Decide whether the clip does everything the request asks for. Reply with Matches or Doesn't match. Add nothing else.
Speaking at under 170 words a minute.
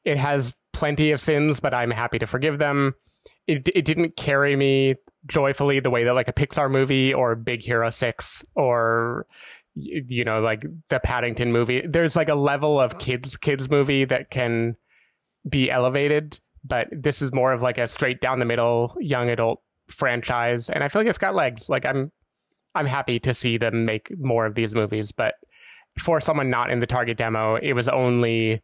Doesn't match